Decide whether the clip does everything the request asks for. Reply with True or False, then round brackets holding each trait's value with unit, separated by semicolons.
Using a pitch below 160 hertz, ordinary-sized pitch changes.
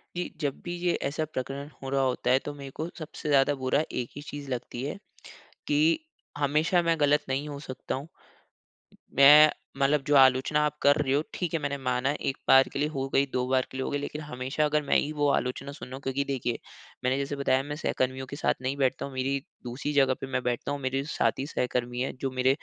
False (140 Hz; 2.0 semitones)